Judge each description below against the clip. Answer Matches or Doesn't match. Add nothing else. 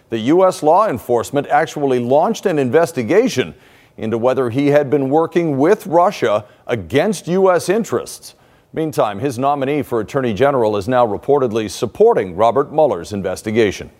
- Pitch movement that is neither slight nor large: Matches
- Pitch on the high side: Doesn't match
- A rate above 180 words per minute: Doesn't match